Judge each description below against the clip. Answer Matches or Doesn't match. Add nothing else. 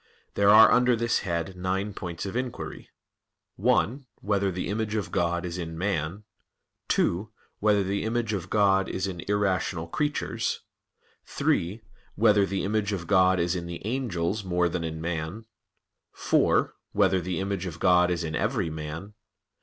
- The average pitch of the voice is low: Matches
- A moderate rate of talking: Matches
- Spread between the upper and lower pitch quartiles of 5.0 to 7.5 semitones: Doesn't match